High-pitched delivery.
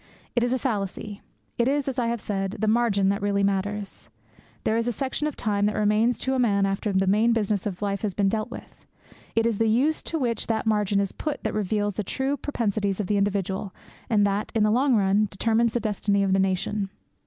Yes: high, 210 Hz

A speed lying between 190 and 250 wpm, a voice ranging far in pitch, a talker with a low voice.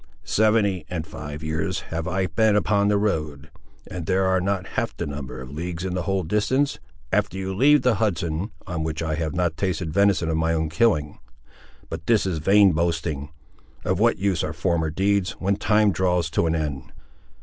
No: average, 195 wpm; average, 3.9 semitones; very low, 90 Hz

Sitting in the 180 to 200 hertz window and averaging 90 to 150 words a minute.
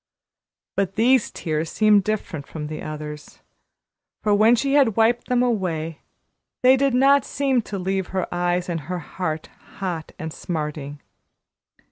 Yes: high, 190 Hz; average, 145 wpm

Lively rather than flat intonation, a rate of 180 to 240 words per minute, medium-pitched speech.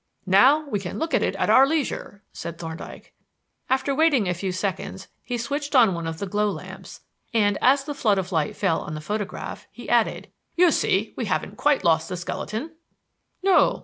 No: wide, 7.5 semitones; average, 195 wpm; high, 210 Hz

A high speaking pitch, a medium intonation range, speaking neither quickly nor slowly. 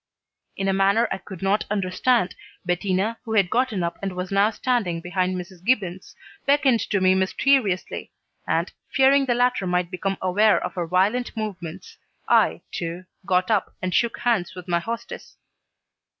Yes: high, 195 Hz; average, 3.9 semitones; average, 165 wpm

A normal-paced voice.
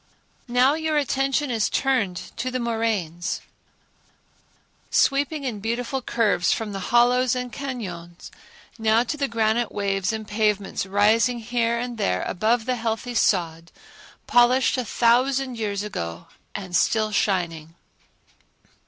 No: slow, 125 wpm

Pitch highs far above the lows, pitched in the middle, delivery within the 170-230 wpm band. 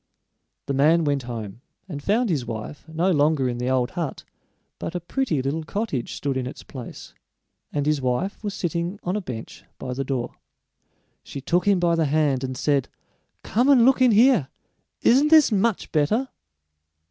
Yes: wide, 7.1 semitones; medium, 155 Hz; average, 180 wpm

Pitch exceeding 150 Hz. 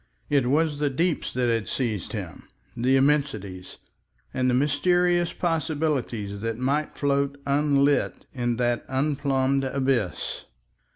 No: low, 135 Hz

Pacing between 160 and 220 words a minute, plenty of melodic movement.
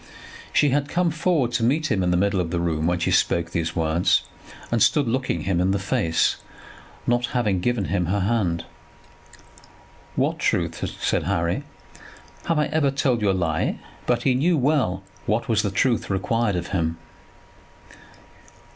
Yes: average, 170 wpm; wide, 6.2 semitones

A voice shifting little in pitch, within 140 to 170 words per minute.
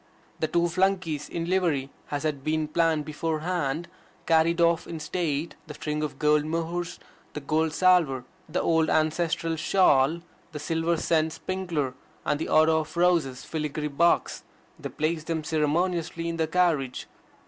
Yes: narrow, 2.0 semitones; average, 150 wpm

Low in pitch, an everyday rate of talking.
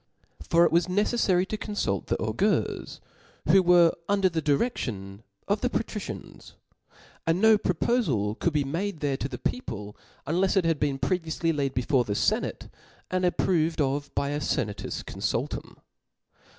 No: medium, 165 Hz; average, 160 wpm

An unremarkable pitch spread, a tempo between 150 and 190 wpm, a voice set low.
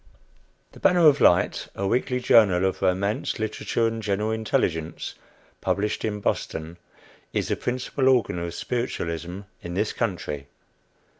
No: average, 4.8 semitones; slow, 135 wpm; low, 105 Hz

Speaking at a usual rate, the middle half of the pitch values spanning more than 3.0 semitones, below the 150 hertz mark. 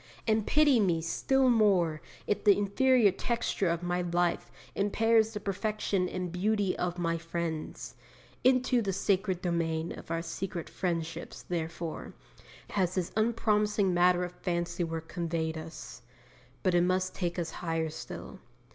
No: average, 145 wpm; average, 3.6 semitones; medium, 180 Hz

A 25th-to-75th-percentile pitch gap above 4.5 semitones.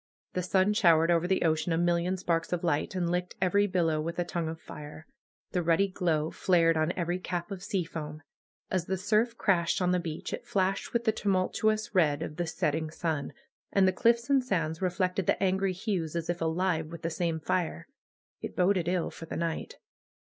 No: narrow, 2.5 semitones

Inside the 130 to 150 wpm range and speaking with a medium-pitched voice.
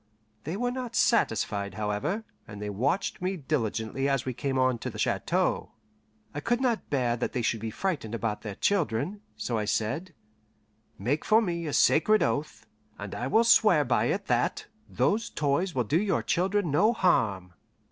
No: average, 180 wpm; medium, 145 Hz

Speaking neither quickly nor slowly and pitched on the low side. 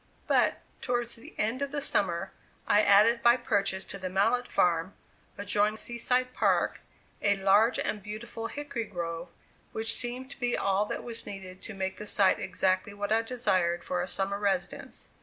No: average, 175 wpm; high, 205 Hz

